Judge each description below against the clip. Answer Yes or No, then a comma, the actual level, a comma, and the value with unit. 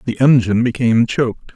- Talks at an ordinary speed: Yes, average, 155 wpm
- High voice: No, low, 120 Hz